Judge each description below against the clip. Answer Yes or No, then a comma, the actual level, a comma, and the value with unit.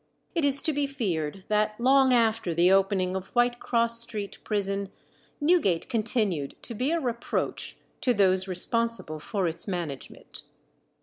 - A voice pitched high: Yes, high, 215 Hz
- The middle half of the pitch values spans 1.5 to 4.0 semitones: No, average, 4.5 semitones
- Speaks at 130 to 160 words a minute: Yes, average, 145 wpm